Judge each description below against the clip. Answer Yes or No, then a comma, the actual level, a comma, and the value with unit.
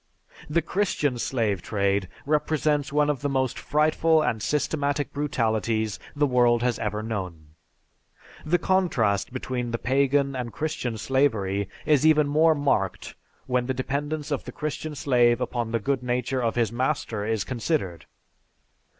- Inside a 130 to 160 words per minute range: Yes, average, 145 wpm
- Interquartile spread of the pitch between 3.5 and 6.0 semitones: Yes, average, 4.5 semitones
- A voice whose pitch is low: Yes, low, 130 Hz